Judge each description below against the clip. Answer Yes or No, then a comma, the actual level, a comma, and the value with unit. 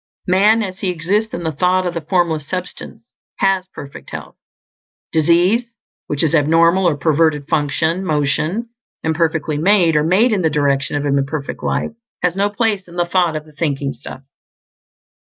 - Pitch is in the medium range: Yes, medium, 165 Hz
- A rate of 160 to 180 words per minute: Yes, average, 165 wpm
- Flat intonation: No, average, 3.7 semitones